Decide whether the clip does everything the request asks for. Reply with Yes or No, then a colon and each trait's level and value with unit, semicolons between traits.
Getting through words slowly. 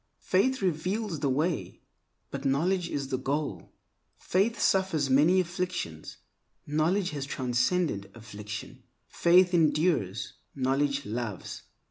Yes: slow, 105 wpm